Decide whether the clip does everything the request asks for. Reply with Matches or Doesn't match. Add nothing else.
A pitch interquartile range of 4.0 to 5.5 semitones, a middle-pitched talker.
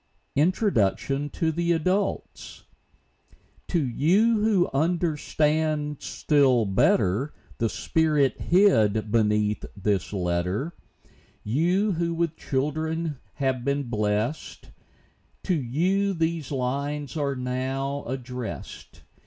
Matches